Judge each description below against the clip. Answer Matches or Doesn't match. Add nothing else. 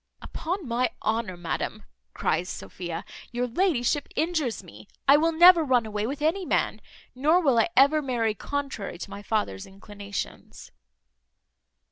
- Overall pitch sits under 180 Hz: Doesn't match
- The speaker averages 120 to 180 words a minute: Matches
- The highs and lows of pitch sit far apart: Matches